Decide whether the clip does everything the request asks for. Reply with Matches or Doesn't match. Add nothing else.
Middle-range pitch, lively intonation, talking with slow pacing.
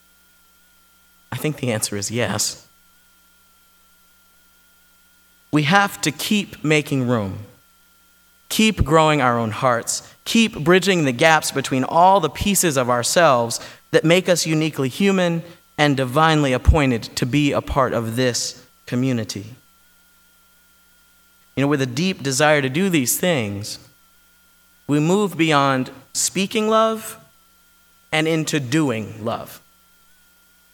Matches